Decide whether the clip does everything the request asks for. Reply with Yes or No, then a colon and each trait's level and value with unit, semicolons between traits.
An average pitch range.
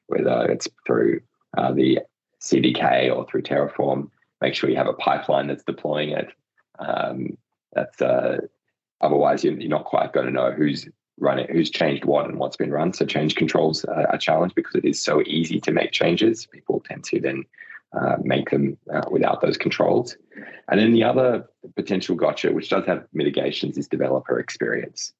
No: wide, 7.1 semitones